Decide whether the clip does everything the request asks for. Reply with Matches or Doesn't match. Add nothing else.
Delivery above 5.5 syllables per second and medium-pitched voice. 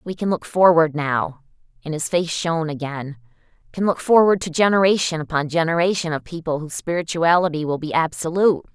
Matches